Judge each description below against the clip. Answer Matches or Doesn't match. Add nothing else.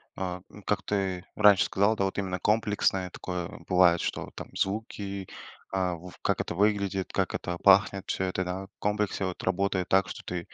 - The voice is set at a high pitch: Doesn't match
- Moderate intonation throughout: Doesn't match